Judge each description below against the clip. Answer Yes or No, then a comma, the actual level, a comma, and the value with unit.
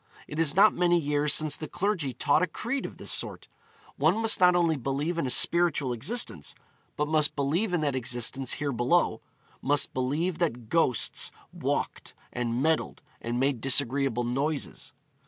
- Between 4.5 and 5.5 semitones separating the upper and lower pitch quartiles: Yes, average, 4.8 semitones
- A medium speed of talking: Yes, average, 165 wpm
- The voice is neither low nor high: Yes, medium, 145 Hz